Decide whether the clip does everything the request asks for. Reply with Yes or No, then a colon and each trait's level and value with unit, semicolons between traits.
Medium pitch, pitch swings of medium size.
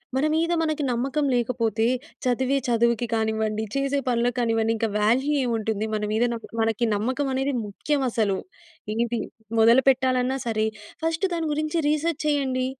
No: high, 245 Hz; average, 3.6 semitones